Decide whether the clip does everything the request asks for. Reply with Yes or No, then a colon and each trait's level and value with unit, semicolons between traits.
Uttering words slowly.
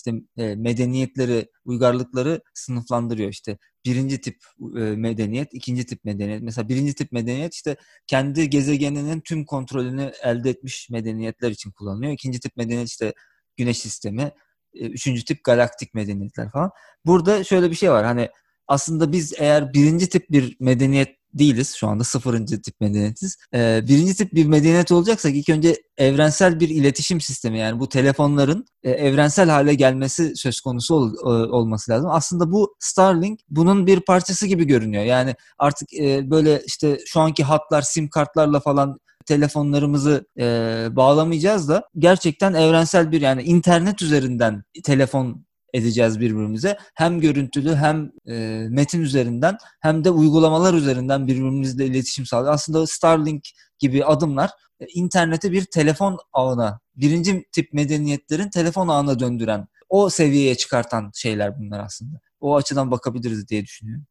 No: average, 135 wpm